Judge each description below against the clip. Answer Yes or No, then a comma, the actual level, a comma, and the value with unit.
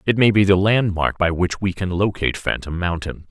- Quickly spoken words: Yes, fast, 220 wpm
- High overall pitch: No, very low, 95 Hz